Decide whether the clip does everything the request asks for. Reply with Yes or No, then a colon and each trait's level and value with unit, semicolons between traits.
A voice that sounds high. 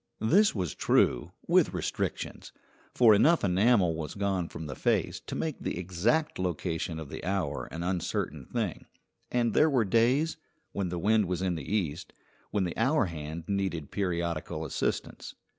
No: very low, 95 Hz